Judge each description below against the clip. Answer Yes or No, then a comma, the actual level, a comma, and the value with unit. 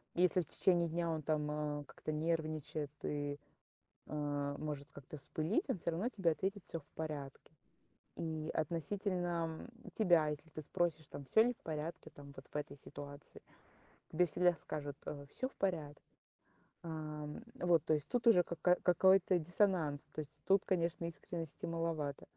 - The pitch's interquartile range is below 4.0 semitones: Yes, average, 3.0 semitones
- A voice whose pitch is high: No, medium, 160 Hz